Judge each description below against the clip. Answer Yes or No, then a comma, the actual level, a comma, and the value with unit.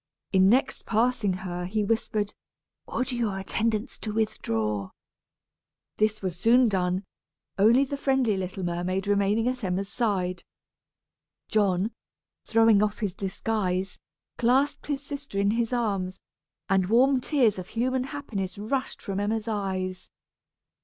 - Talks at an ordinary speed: No, slow, 130 wpm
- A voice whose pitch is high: Yes, high, 210 Hz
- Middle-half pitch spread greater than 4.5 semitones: No, average, 3.9 semitones